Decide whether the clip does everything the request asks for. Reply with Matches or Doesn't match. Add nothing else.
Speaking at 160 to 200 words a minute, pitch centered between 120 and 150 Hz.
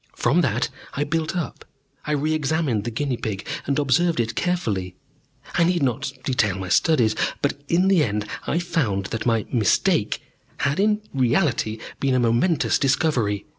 Matches